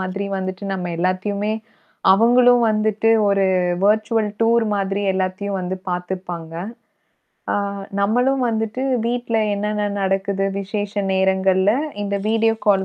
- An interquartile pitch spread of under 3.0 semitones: Yes, narrow, 2.5 semitones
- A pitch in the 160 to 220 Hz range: Yes, high, 200 Hz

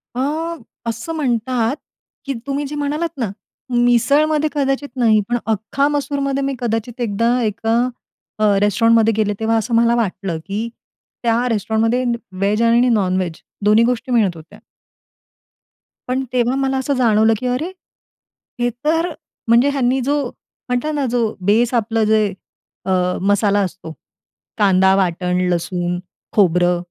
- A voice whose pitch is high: Yes, high, 230 Hz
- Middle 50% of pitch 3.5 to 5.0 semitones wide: Yes, average, 4.1 semitones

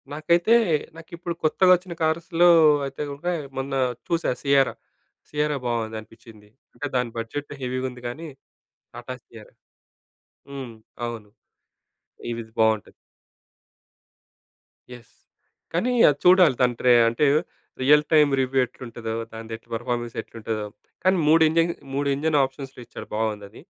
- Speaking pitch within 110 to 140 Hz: Yes, low, 135 Hz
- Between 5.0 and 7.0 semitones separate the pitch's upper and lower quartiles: Yes, wide, 5.4 semitones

